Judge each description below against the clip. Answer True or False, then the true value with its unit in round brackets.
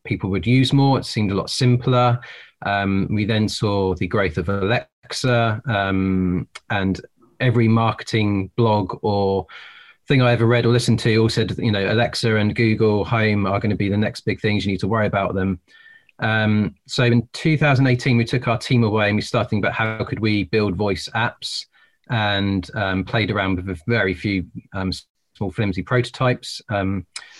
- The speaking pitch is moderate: False (110 Hz)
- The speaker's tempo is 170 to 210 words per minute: True (185 wpm)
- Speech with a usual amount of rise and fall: True (3.4 semitones)